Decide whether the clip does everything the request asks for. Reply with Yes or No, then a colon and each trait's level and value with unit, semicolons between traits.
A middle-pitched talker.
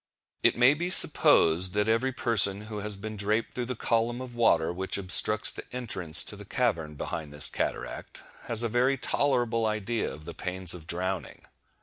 No: low, 105 Hz